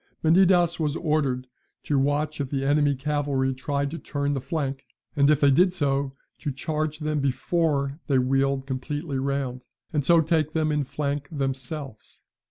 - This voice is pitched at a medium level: Yes, medium, 145 Hz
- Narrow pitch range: Yes, narrow, 2.1 semitones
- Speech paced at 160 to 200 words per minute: Yes, average, 165 wpm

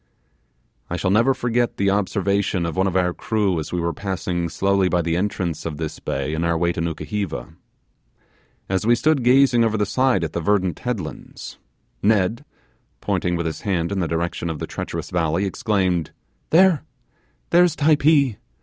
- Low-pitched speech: Yes, very low, 95 Hz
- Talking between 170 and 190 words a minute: Yes, average, 175 wpm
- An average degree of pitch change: Yes, average, 5.0 semitones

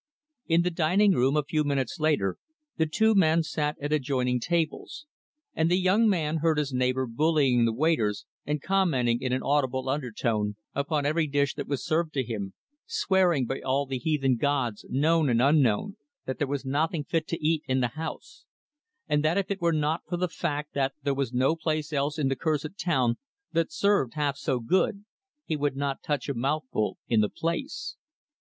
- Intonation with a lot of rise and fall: No, average, 3.8 semitones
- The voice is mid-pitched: Yes, medium, 145 Hz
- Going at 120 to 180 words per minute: No, average, 190 wpm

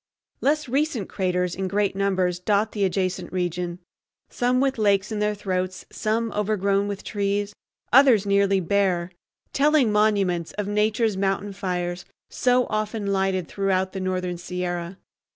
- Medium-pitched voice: No, high, 200 Hz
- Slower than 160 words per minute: Yes, slow, 135 wpm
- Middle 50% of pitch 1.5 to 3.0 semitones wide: Yes, narrow, 2.5 semitones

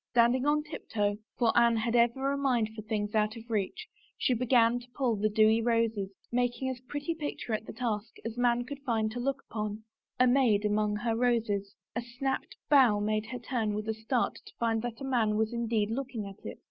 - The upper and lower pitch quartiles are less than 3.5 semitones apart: Yes, narrow, 2.6 semitones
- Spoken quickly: Yes, fast, 225 wpm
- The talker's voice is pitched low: No, high, 230 Hz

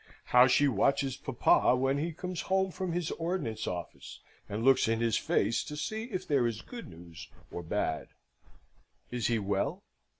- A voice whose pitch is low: Yes, low, 130 Hz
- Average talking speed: Yes, average, 170 wpm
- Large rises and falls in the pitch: Yes, wide, 7.5 semitones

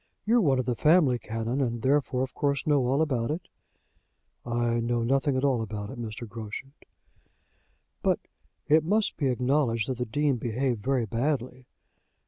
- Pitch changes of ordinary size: Yes, average, 3.3 semitones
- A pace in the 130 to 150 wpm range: No, average, 165 wpm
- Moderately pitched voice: No, low, 130 Hz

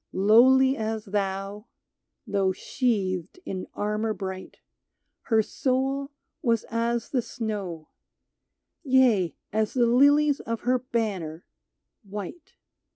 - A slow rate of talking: Yes, slow, 105 wpm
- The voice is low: No, high, 220 Hz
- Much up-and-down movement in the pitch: No, average, 4.5 semitones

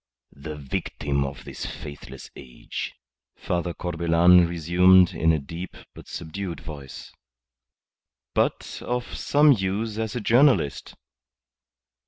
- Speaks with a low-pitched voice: Yes, very low, 85 Hz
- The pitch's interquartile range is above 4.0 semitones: Yes, average, 4.7 semitones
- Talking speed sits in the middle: No, slow, 110 wpm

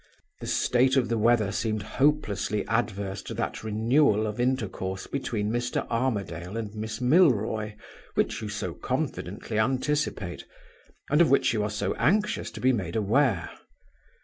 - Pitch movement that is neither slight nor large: Yes, average, 3.8 semitones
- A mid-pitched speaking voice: No, low, 110 Hz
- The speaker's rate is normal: Yes, average, 150 wpm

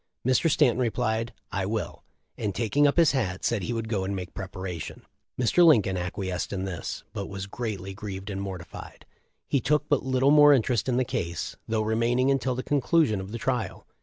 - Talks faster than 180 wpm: Yes, average, 195 wpm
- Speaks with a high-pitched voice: No, low, 110 Hz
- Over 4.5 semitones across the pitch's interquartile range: Yes, average, 5.2 semitones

